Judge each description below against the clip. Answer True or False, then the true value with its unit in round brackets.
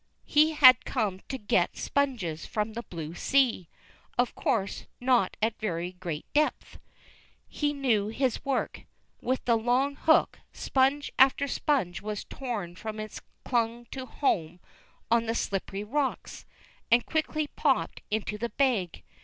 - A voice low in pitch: False (235 Hz)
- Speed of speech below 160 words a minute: True (140 wpm)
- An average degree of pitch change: True (4.9 semitones)